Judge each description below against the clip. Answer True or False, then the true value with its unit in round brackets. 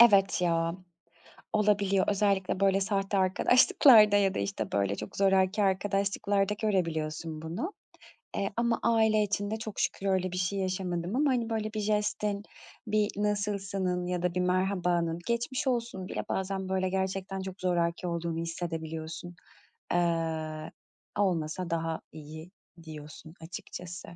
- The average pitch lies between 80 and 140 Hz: False (190 Hz)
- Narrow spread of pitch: False (3.3 semitones)